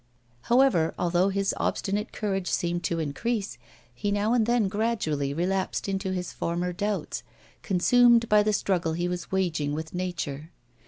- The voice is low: No, high, 190 Hz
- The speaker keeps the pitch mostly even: No, average, 3.7 semitones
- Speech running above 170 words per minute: No, average, 150 wpm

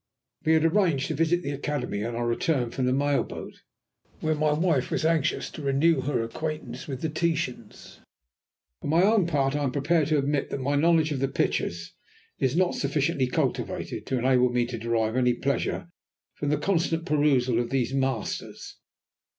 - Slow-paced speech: No, average, 185 wpm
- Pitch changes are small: No, average, 3.8 semitones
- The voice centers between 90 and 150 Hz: Yes, medium, 140 Hz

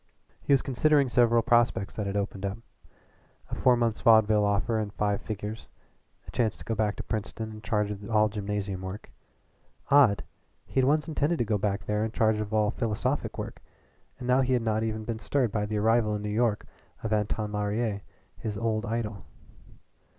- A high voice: No, low, 110 Hz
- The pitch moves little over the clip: Yes, narrow, 2.2 semitones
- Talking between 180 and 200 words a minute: Yes, average, 195 wpm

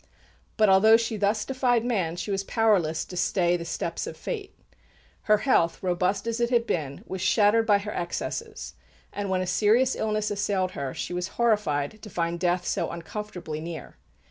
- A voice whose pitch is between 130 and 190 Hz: No, high, 200 Hz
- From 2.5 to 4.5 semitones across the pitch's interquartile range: Yes, average, 3.9 semitones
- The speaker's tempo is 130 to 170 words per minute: No, average, 180 wpm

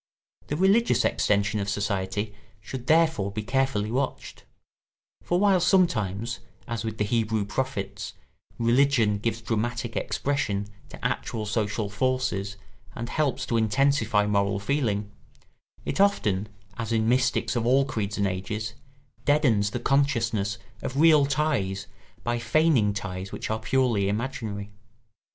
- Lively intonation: No, average, 4.6 semitones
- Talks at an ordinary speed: No, slow, 130 wpm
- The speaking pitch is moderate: No, low, 115 Hz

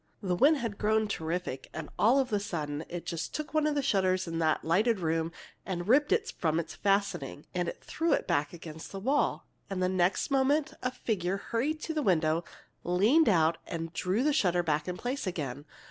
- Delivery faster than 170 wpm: Yes, fast, 205 wpm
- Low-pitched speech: No, medium, 185 Hz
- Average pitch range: No, wide, 7.2 semitones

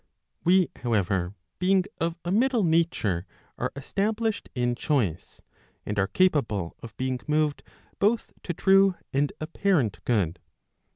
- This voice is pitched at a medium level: Yes, medium, 150 Hz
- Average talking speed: No, slow, 125 wpm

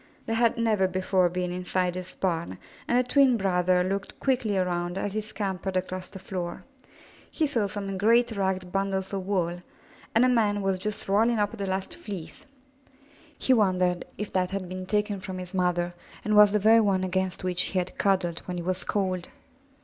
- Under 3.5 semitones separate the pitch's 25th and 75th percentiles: Yes, narrow, 2.4 semitones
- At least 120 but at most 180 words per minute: No, average, 190 wpm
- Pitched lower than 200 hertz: Yes, high, 190 Hz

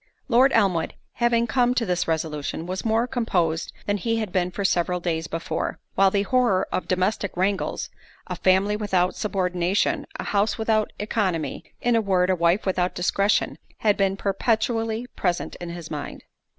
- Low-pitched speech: No, high, 195 Hz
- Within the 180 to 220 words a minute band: No, average, 155 wpm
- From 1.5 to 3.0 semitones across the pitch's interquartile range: No, average, 3.7 semitones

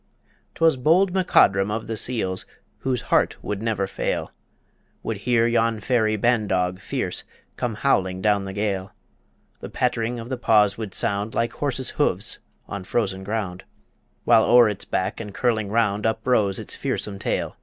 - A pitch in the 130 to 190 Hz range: No, low, 110 Hz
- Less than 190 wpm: Yes, average, 160 wpm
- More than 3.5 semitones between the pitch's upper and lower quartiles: No, average, 3.2 semitones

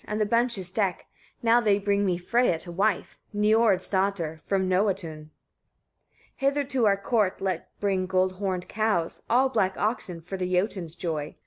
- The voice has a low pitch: No, high, 195 Hz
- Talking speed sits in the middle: Yes, average, 165 wpm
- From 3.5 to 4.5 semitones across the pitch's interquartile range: No, average, 3.0 semitones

